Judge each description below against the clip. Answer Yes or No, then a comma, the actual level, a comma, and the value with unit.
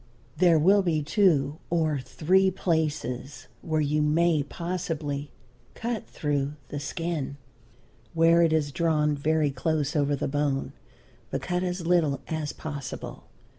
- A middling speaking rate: No, slow, 130 wpm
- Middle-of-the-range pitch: Yes, medium, 155 Hz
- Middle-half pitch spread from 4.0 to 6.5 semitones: No, average, 2.8 semitones